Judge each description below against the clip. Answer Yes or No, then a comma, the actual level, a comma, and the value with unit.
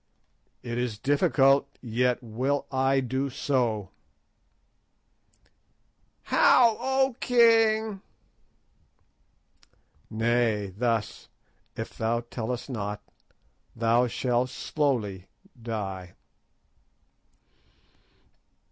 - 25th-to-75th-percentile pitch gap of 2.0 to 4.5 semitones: Yes, average, 3.8 semitones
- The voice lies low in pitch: Yes, low, 125 Hz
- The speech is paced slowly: Yes, slow, 65 wpm